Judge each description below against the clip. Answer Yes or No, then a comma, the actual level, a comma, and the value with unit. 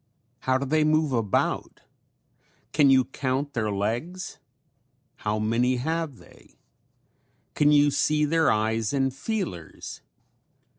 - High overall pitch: No, low, 135 Hz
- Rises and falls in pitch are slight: No, average, 4.9 semitones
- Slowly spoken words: Yes, slow, 115 wpm